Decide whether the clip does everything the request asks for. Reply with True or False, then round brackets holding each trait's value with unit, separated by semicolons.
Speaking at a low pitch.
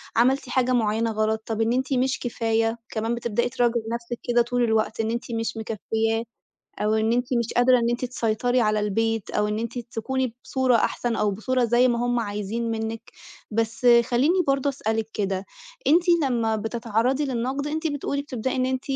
False (235 Hz)